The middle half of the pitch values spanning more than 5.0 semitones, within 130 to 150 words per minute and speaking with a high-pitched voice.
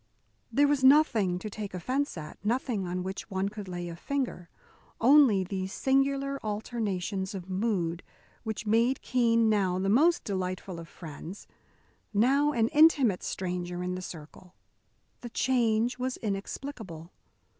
Yes: wide, 5.6 semitones; average, 140 wpm; high, 210 Hz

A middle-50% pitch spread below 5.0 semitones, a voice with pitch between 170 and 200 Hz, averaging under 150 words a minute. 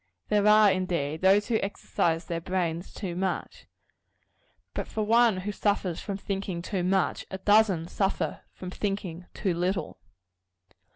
Yes: average, 2.7 semitones; high, 190 Hz; average, 140 wpm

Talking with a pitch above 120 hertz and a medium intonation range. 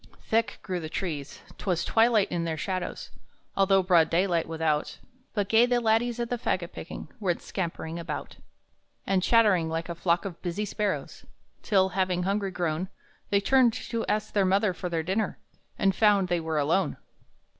Yes: medium, 185 Hz; average, 3.7 semitones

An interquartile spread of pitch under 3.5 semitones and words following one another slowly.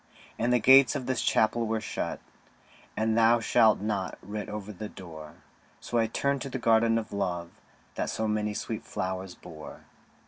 No: average, 3.0 semitones; average, 175 wpm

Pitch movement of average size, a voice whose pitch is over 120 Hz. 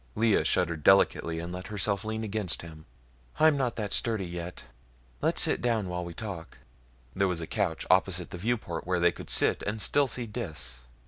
No: average, 4.2 semitones; very low, 95 Hz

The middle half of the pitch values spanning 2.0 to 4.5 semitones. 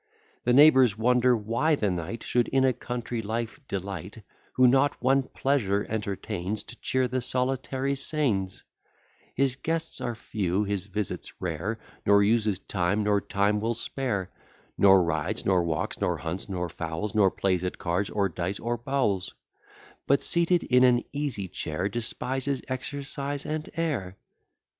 No: average, 5.2 semitones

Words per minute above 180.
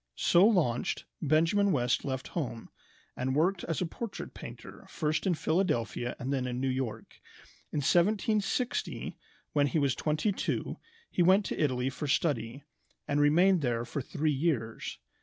No: average, 155 wpm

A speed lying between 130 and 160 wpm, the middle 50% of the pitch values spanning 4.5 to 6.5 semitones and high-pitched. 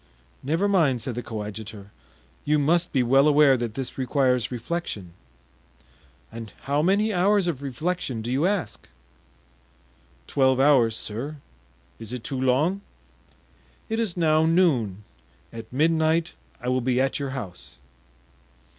No: slow, 135 wpm; wide, 5.4 semitones; low, 135 Hz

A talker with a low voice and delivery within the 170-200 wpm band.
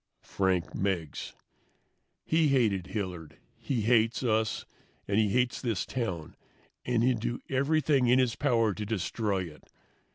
No: low, 110 Hz; slow, 135 wpm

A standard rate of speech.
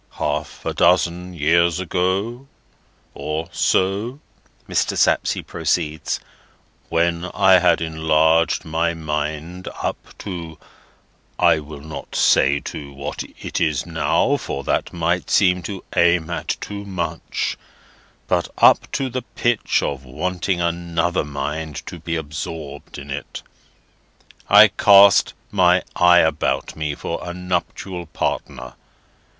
No: slow, 120 wpm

